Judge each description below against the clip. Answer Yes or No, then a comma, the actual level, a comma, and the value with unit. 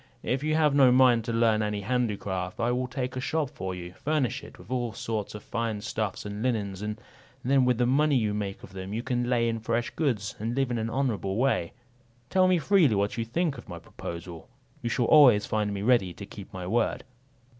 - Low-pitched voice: Yes, low, 115 Hz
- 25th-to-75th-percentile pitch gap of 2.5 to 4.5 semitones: Yes, average, 3.9 semitones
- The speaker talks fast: Yes, fast, 225 wpm